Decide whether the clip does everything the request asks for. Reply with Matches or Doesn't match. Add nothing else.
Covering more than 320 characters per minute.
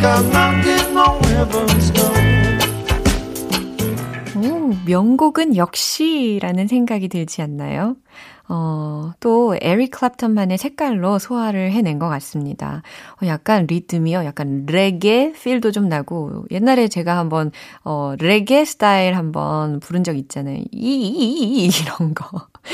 Doesn't match